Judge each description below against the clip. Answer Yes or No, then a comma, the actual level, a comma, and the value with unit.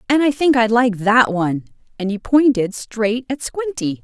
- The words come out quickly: No, average, 195 wpm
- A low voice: No, high, 235 Hz